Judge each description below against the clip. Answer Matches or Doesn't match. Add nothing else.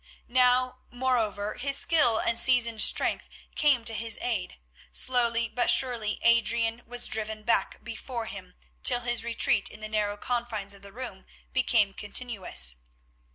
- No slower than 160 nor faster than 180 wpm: Doesn't match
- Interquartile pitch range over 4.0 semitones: Doesn't match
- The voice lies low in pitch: Doesn't match